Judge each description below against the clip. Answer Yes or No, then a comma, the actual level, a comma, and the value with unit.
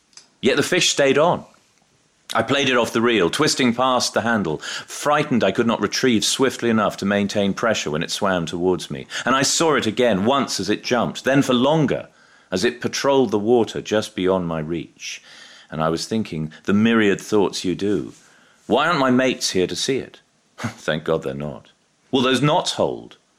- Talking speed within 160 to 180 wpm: No, average, 195 wpm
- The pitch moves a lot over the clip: Yes, wide, 6.1 semitones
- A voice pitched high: No, low, 105 Hz